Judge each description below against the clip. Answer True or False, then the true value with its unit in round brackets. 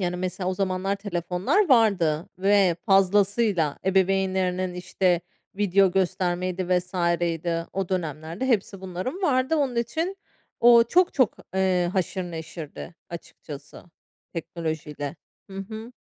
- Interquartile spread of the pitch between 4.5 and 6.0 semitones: False (2.7 semitones)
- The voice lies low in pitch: False (185 Hz)